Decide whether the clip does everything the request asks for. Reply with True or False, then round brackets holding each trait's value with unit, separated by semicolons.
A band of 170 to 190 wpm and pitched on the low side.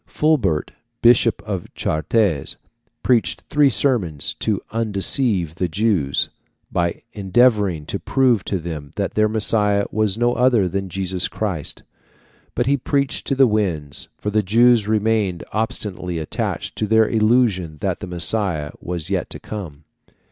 False (140 wpm; 105 Hz)